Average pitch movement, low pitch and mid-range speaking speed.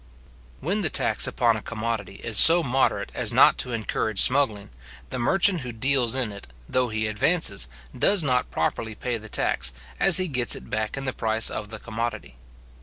Yes: average, 3.9 semitones; low, 120 Hz; average, 185 wpm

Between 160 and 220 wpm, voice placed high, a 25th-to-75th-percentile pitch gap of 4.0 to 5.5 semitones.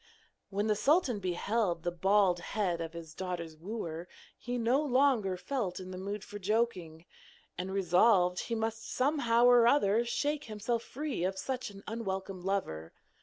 Yes: average, 165 wpm; high, 205 Hz; average, 4.6 semitones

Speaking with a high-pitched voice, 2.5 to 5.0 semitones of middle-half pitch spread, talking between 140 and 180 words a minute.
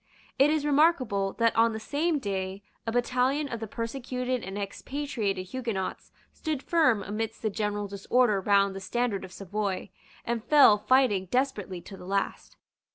Yes: high, 225 Hz; average, 4.6 semitones; average, 160 wpm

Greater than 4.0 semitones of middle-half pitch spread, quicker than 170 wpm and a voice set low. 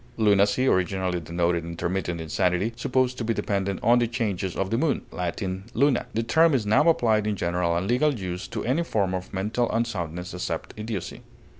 Yes: average, 4.7 semitones; average, 180 wpm; low, 100 Hz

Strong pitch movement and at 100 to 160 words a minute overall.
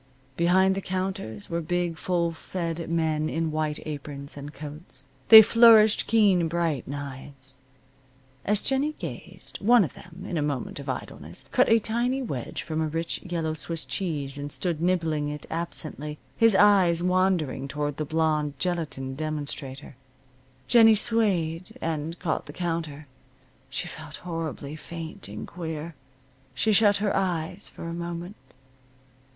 No: average, 3.7 semitones; average, 145 wpm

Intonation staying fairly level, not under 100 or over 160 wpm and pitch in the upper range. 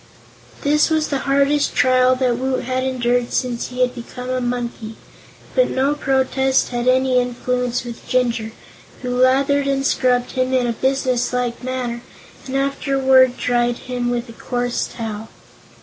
Yes: narrow, 1.5 semitones; average, 150 wpm; very high, 255 Hz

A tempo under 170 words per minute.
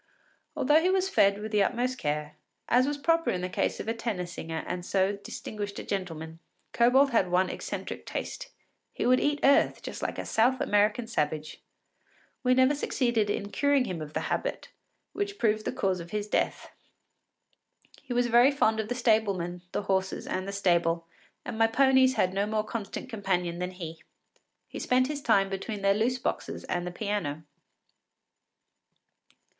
No: average, 175 wpm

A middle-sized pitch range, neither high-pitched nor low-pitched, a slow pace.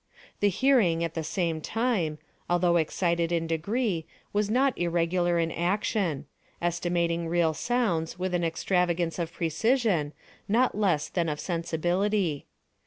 Yes: average, 3.3 semitones; medium, 175 Hz; slow, 125 wpm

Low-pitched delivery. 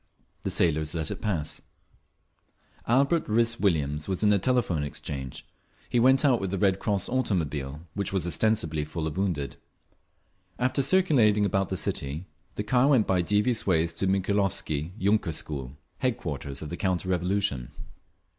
Yes: very low, 95 Hz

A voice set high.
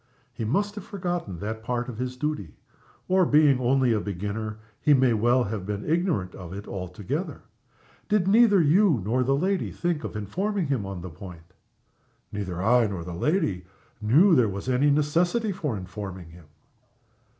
No: low, 120 Hz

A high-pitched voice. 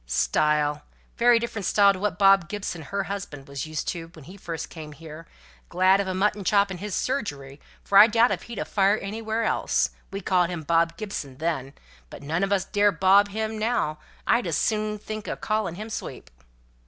Yes: high, 195 Hz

